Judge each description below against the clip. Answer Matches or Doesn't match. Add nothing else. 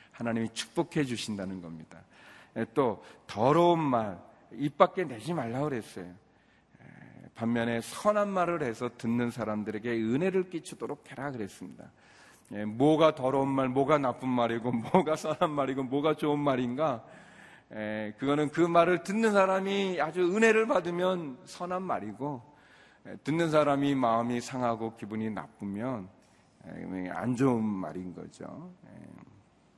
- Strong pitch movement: Matches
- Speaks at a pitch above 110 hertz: Matches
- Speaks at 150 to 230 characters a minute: Doesn't match